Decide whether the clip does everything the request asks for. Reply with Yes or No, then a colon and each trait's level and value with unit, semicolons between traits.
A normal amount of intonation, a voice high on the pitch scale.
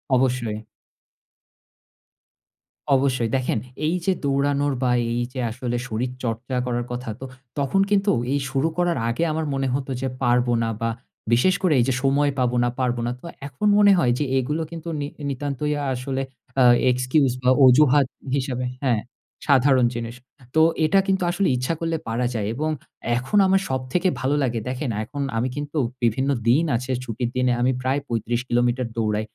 No: average, 3.0 semitones; low, 130 Hz